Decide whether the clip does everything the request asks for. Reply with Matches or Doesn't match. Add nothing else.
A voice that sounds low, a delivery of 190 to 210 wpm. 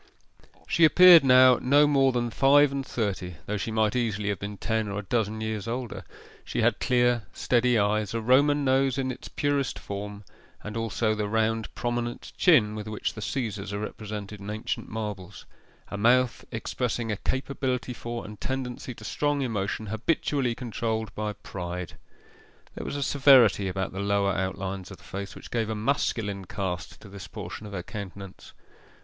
Doesn't match